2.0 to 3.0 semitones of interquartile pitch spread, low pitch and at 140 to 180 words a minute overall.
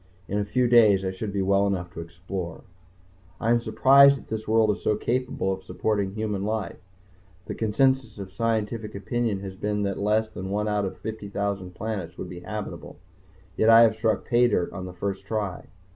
No: narrow, 2.5 semitones; low, 105 Hz; average, 190 wpm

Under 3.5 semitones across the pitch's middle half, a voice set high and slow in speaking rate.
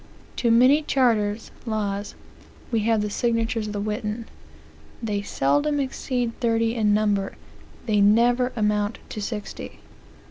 Yes: narrow, 2.4 semitones; high, 225 Hz; slow, 130 wpm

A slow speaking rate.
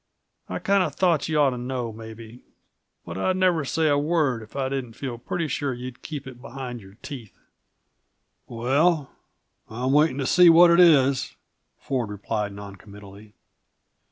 No: average, 160 wpm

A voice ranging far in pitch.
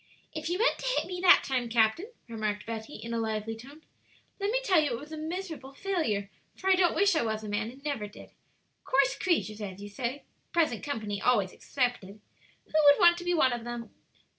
Yes: wide, 7.5 semitones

